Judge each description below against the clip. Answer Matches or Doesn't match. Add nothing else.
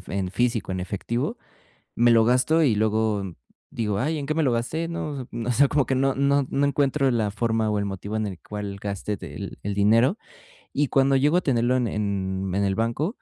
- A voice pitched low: Matches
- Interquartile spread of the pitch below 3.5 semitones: Doesn't match